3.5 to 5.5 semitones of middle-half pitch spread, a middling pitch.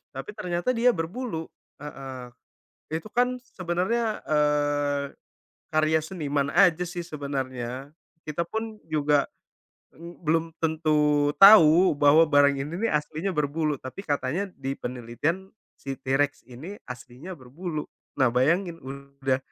Yes: average, 3.9 semitones; medium, 150 Hz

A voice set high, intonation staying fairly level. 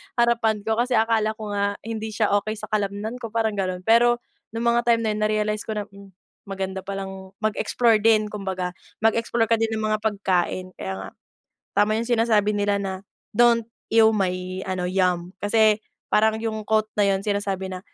Yes: high, 215 Hz; narrow, 2.3 semitones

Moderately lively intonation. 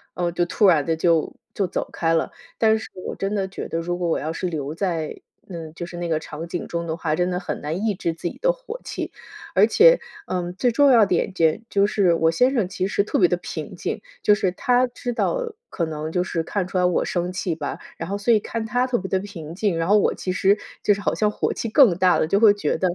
Yes: average, 3.9 semitones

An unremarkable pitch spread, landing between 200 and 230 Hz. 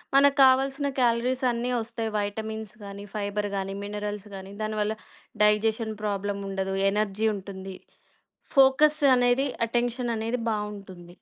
Yes: average, 3.2 semitones; high, 215 Hz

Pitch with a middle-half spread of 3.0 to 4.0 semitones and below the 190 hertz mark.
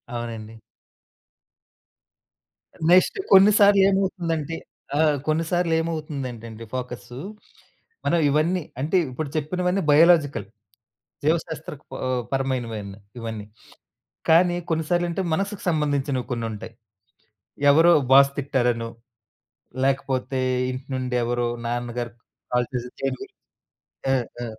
No: average, 5.3 semitones; medium, 140 Hz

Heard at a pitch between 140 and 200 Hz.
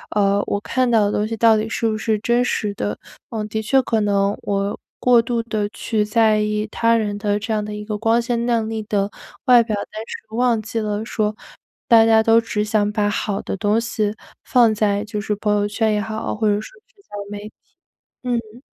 No: high, 215 Hz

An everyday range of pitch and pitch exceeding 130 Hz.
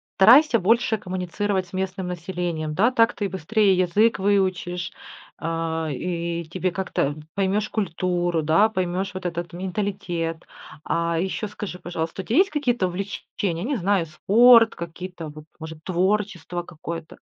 Yes: average, 3.2 semitones; medium, 185 Hz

